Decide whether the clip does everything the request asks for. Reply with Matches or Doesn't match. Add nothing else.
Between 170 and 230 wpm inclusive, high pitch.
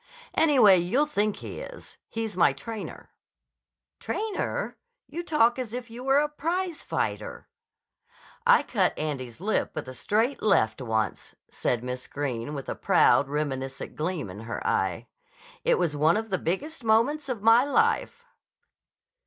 Doesn't match